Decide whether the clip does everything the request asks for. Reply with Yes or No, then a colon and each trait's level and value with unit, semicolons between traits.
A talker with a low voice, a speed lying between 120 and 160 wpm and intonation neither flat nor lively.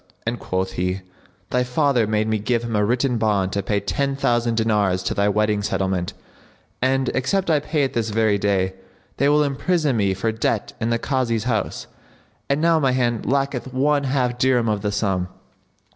No: low, 115 Hz; average, 190 wpm; average, 4.4 semitones